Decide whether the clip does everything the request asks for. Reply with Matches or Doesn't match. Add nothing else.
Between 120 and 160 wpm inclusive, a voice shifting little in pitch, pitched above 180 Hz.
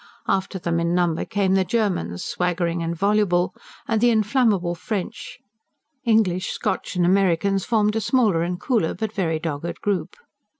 Doesn't match